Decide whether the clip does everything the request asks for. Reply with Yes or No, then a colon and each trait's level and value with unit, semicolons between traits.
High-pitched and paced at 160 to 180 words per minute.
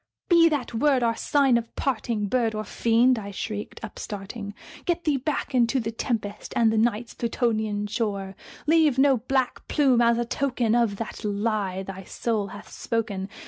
Yes: high, 230 Hz; average, 170 wpm